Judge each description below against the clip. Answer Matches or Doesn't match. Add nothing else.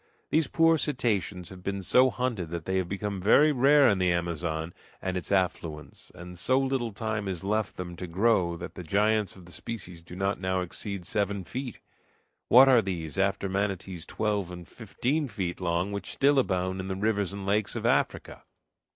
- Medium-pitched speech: Doesn't match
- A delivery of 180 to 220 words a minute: Matches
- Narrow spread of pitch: Doesn't match